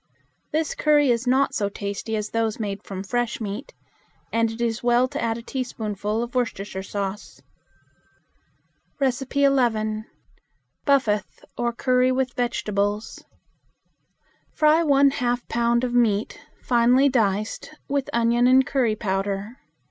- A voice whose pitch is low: No, high, 235 Hz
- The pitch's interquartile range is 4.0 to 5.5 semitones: No, average, 3.3 semitones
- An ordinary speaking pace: No, slow, 125 wpm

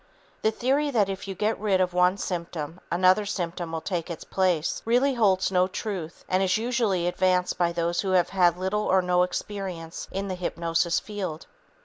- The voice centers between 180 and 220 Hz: Yes, medium, 185 Hz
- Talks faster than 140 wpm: Yes, average, 190 wpm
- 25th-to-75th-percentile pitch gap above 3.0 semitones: No, narrow, 2.6 semitones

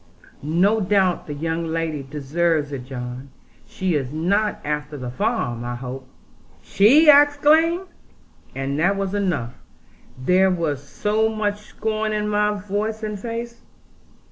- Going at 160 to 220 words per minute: No, average, 140 wpm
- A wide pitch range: Yes, wide, 6.9 semitones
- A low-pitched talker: No, medium, 185 Hz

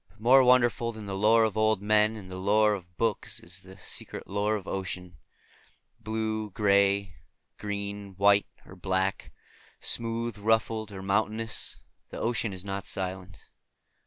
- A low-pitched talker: Yes, low, 105 Hz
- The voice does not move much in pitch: Yes, narrow, 2.3 semitones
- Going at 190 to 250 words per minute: No, average, 150 wpm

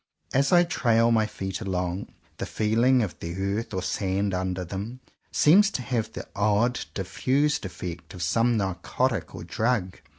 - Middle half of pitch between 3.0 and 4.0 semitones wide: No, average, 4.6 semitones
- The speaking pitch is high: No, low, 105 Hz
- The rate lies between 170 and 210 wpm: No, average, 160 wpm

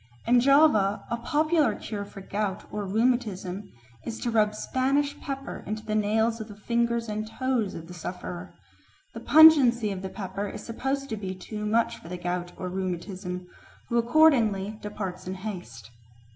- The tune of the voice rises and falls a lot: No, average, 3.8 semitones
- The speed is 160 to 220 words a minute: Yes, average, 170 wpm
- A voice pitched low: No, high, 215 Hz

